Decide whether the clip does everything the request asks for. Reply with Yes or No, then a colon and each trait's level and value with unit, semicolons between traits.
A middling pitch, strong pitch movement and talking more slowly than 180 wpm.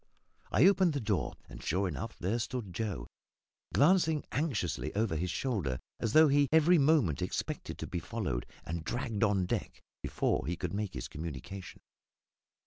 No: low, 105 Hz; wide, 8.2 semitones; average, 160 wpm